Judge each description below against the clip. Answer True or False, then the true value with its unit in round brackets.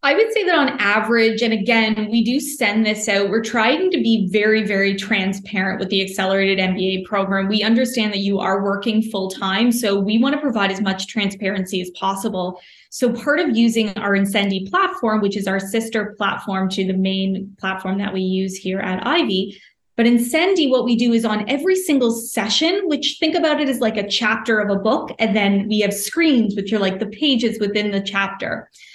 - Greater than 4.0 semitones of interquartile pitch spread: False (3.3 semitones)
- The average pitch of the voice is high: True (215 Hz)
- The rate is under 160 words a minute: False (205 wpm)